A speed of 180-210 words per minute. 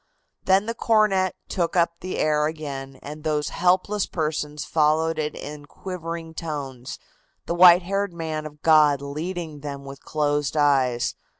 No: average, 145 wpm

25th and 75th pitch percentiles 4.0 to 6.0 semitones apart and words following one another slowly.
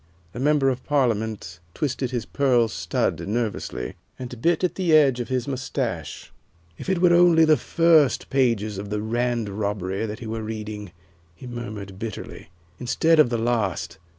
No: average, 4.5 semitones; average, 165 wpm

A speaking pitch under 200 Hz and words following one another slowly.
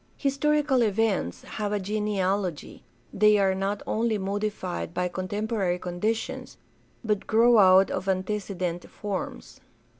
No: high, 205 Hz; slow, 120 wpm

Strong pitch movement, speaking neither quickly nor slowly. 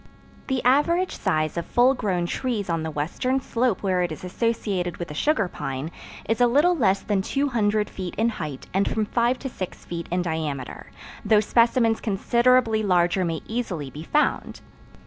Yes: wide, 5.8 semitones; average, 175 wpm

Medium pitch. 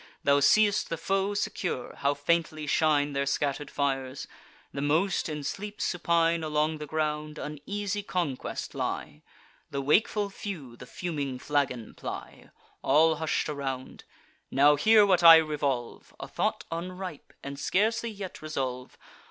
Yes: medium, 155 Hz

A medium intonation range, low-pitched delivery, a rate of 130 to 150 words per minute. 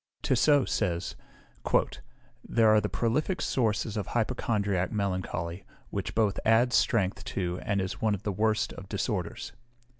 Yes: average, 3.2 semitones; low, 105 Hz; average, 140 wpm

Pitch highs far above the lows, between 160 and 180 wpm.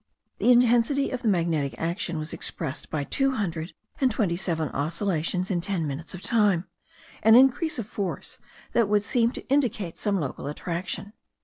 Yes: wide, 5.8 semitones; average, 170 wpm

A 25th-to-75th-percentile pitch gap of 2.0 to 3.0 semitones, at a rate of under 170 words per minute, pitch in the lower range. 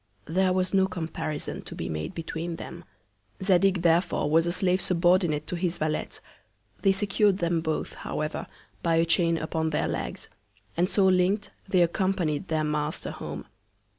No: narrow, 2.6 semitones; average, 160 wpm; medium, 170 Hz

